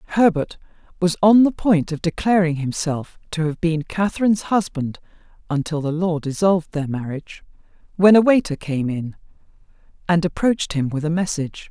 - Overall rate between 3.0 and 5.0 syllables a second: No, 5.4 syllables/s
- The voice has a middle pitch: Yes, medium, 170 Hz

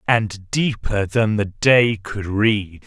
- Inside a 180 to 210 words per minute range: No, average, 145 wpm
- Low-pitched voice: Yes, low, 105 Hz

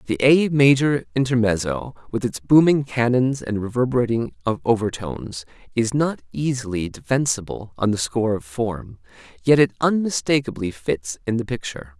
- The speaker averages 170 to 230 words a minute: No, slow, 135 wpm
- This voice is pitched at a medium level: No, low, 115 Hz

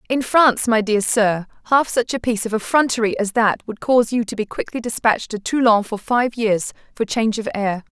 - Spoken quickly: Yes, fast, 220 wpm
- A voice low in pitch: No, high, 225 Hz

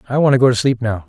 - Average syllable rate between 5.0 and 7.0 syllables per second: No, 7.9 syllables/s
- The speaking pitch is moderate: No, low, 125 Hz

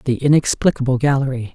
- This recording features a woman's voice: Yes, female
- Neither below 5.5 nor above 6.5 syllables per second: Yes, 6.0 syllables/s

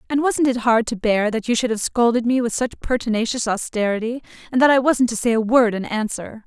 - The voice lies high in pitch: Yes, high, 235 Hz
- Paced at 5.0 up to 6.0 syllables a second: Yes, 5.8 syllables/s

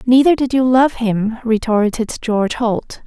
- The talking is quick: No, average, 155 wpm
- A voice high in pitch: Yes, high, 235 Hz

